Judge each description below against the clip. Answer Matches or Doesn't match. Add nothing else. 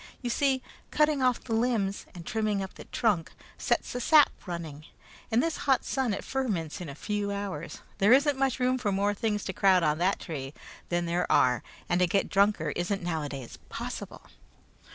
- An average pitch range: Doesn't match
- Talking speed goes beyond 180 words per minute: Matches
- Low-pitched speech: Doesn't match